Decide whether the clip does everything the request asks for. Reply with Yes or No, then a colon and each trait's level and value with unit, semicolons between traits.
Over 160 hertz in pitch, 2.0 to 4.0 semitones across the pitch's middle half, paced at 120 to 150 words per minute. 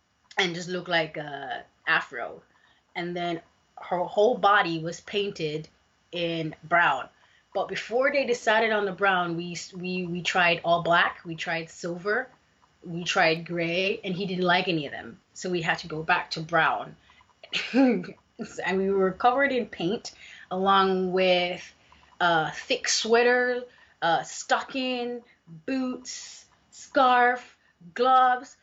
No: medium, 185 Hz; average, 5.3 semitones; average, 140 wpm